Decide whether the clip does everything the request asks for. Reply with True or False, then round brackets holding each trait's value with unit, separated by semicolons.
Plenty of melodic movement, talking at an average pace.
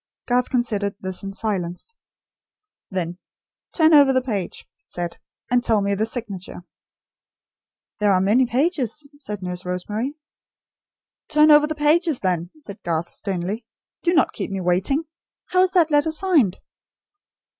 True (7.9 semitones; 145 wpm)